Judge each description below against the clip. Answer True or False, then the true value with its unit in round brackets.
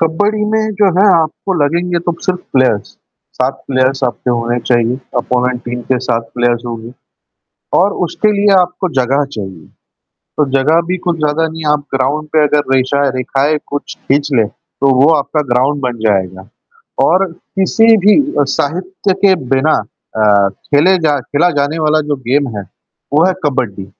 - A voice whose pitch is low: False (145 Hz)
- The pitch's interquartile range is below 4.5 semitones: False (5.3 semitones)